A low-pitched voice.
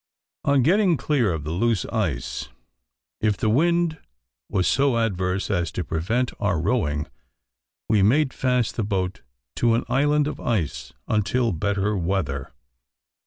Yes: low, 110 Hz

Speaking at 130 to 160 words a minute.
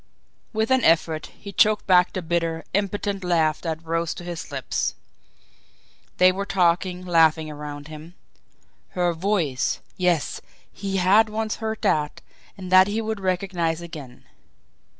Yes: average, 140 wpm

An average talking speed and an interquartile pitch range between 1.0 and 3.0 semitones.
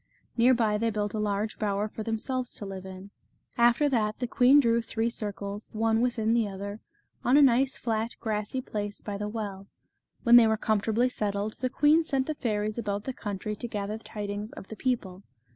Yes: average, 195 wpm; narrow, 2.5 semitones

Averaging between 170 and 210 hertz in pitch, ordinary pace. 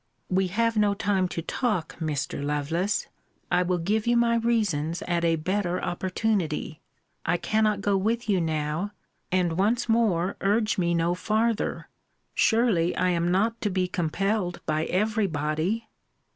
Yes: medium, 185 Hz; average, 150 wpm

